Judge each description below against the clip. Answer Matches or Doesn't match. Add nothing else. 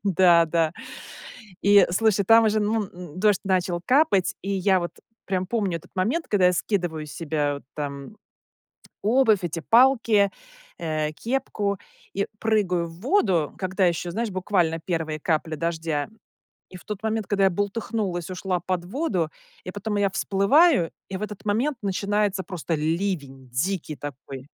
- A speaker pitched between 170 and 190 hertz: Matches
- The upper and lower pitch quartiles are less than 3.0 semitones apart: Doesn't match